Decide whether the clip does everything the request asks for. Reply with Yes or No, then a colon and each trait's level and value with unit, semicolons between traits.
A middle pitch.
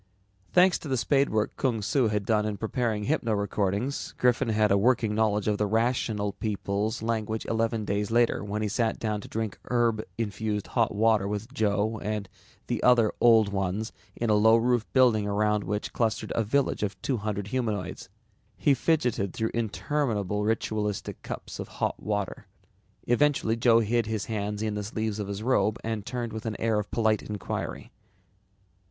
No: low, 110 Hz